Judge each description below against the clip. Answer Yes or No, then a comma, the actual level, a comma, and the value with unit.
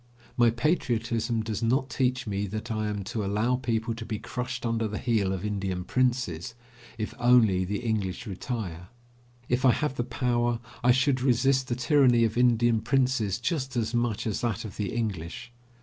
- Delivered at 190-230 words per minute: No, average, 180 wpm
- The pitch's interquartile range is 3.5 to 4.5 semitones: No, average, 2.7 semitones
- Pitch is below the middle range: Yes, low, 115 Hz